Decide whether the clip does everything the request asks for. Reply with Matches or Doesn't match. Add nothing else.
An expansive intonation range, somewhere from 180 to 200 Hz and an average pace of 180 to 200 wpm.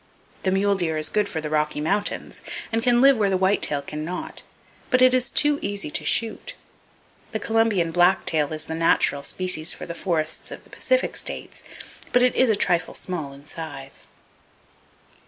Matches